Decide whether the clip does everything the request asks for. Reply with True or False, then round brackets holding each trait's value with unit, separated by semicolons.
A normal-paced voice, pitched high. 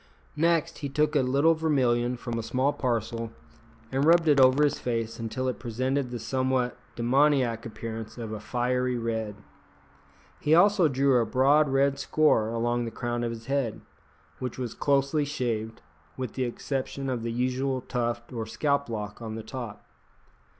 False (165 wpm; 125 Hz)